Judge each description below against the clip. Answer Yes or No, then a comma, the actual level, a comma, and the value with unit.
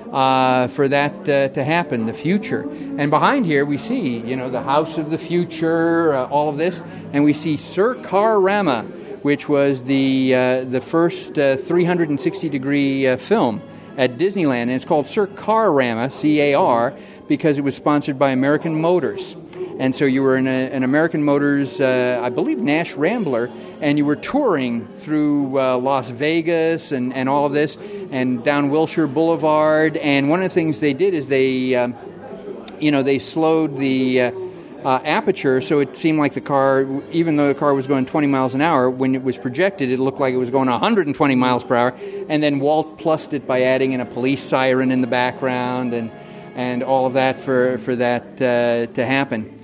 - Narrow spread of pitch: No, average, 3.4 semitones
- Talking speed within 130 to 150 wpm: No, average, 195 wpm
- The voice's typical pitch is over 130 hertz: Yes, medium, 140 Hz